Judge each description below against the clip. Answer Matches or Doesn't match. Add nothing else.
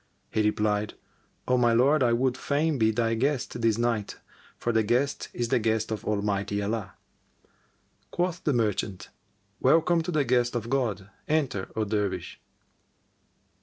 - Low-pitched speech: Matches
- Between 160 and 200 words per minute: Doesn't match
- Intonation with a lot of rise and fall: Doesn't match